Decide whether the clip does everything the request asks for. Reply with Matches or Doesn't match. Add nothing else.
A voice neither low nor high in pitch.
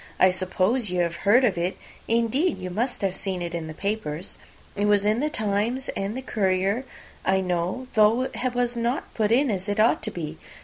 Doesn't match